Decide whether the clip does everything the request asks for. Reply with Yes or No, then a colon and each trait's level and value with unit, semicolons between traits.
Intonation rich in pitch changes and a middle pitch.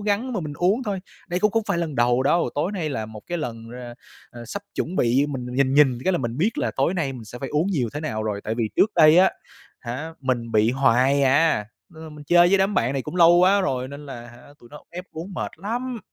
Yes: wide, 6.5 semitones; medium, 150 Hz